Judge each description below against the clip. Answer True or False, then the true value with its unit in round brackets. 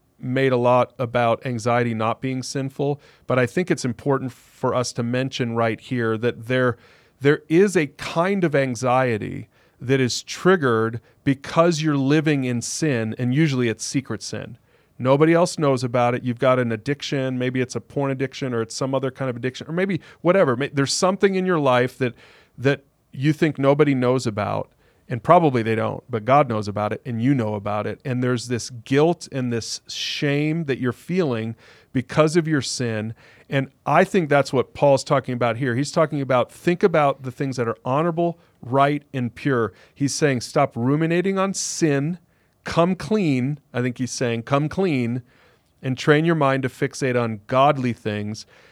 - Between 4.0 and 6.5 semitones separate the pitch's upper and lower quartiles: False (3.5 semitones)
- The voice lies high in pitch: False (130 Hz)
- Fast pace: False (185 wpm)